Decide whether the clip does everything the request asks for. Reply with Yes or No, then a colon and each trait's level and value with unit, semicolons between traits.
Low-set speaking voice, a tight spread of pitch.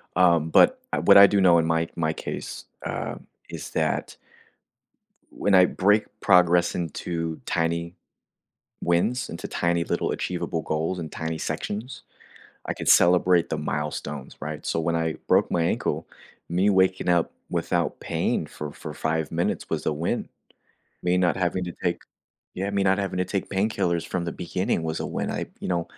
Yes: very low, 85 Hz; narrow, 2.2 semitones